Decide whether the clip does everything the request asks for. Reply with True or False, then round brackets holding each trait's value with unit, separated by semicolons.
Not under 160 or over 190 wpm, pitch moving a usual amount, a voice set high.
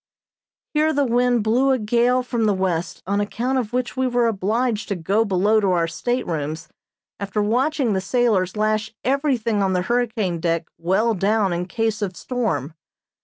True (170 wpm; 4.5 semitones; 215 Hz)